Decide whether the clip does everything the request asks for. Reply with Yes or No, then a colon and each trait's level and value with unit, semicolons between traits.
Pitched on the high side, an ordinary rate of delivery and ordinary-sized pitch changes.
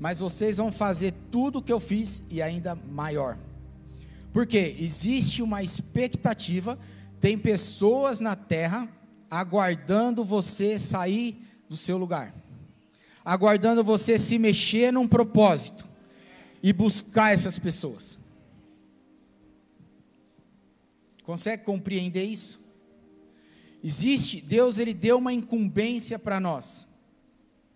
No: high, 205 Hz; slow, 100 wpm; average, 4.8 semitones